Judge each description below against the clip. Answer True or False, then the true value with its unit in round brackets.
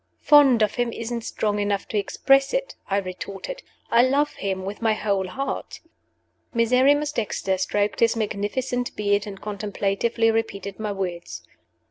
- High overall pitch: True (215 Hz)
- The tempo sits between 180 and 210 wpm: False (145 wpm)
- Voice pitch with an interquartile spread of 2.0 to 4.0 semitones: True (3.6 semitones)